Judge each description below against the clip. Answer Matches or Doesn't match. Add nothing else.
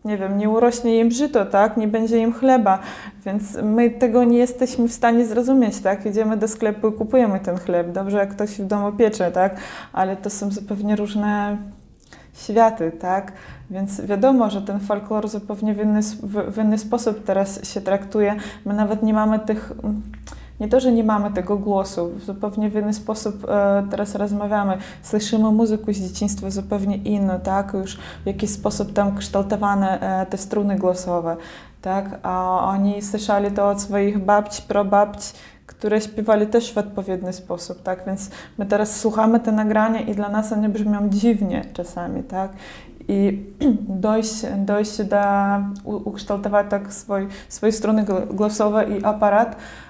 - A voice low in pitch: Doesn't match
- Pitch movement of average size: Doesn't match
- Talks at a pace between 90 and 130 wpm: Doesn't match